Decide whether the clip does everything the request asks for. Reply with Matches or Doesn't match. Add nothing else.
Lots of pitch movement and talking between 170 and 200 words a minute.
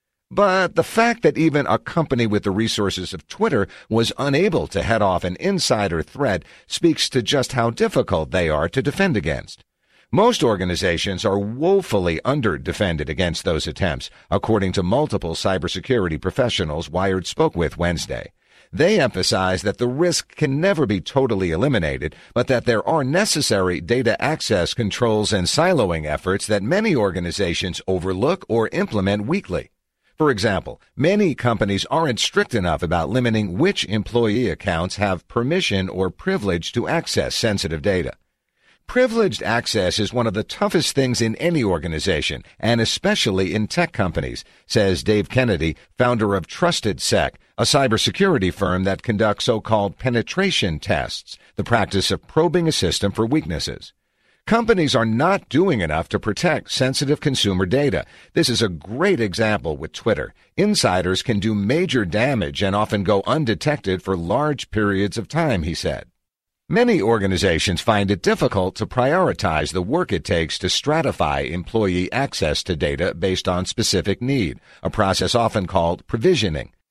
Doesn't match